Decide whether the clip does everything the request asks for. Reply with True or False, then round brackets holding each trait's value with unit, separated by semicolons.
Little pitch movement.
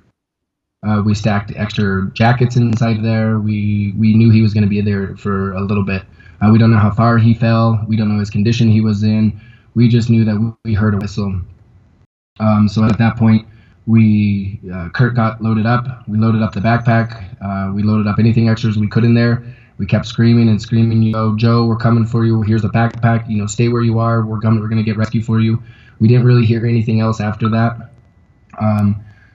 True (1.6 semitones)